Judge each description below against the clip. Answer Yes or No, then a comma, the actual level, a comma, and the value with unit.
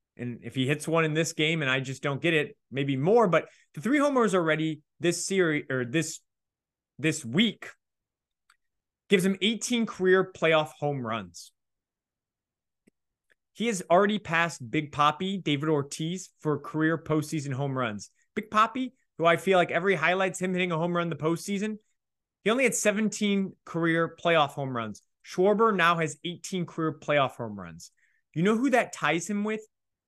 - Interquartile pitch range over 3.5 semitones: Yes, average, 5.0 semitones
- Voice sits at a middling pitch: Yes, medium, 165 Hz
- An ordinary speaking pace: Yes, average, 170 wpm